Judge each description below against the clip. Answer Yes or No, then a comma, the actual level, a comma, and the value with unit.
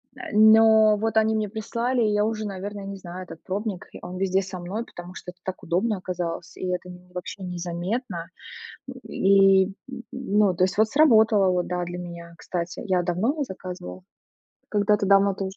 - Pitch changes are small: No, average, 3.2 semitones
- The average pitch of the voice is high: Yes, high, 195 Hz